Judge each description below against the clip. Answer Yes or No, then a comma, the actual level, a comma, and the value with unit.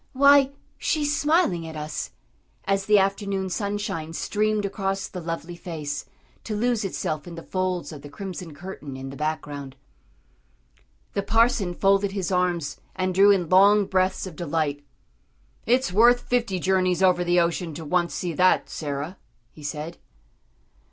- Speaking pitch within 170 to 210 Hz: Yes, medium, 185 Hz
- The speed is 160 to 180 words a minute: No, average, 150 wpm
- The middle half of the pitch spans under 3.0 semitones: No, average, 3.7 semitones